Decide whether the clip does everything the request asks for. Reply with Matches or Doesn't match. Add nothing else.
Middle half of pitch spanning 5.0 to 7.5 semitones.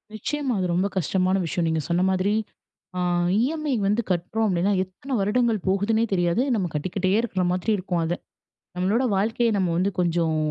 Doesn't match